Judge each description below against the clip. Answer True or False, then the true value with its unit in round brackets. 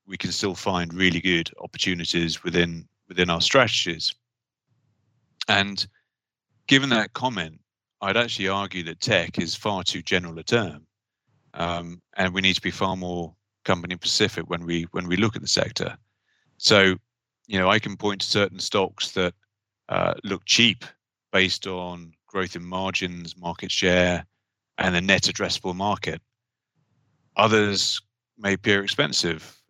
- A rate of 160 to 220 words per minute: False (150 wpm)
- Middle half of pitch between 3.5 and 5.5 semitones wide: True (4.3 semitones)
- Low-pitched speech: True (95 Hz)